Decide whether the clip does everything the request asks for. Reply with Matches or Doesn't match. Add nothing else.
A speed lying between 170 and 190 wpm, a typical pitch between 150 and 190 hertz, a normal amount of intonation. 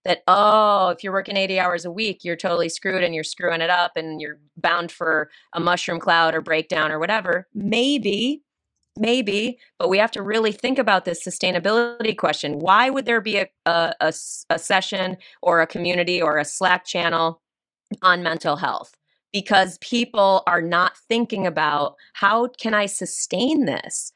Matches